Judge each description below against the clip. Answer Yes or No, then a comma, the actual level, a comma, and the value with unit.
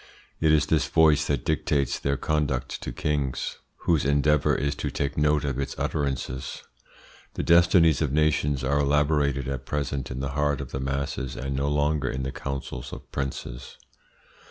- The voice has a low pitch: Yes, very low, 70 Hz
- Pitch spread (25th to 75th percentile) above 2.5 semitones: No, narrow, 1.7 semitones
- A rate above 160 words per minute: Yes, average, 170 wpm